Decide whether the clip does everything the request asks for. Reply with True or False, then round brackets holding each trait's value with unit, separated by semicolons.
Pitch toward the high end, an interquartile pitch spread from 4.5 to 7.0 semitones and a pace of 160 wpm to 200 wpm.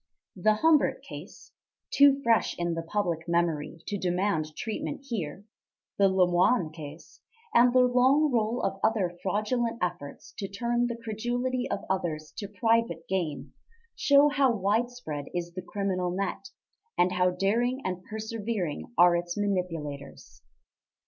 False (200 Hz; 5.2 semitones; 135 wpm)